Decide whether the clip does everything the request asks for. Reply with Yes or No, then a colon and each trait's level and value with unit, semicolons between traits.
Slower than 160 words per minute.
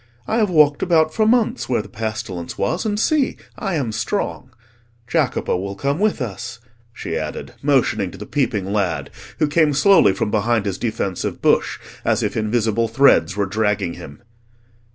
No: average, 170 wpm